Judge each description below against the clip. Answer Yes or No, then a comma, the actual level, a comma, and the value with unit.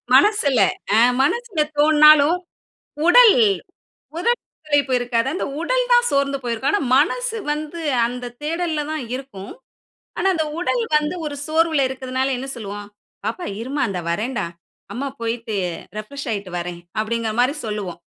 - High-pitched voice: Yes, very high, 275 Hz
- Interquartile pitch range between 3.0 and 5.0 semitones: No, wide, 5.5 semitones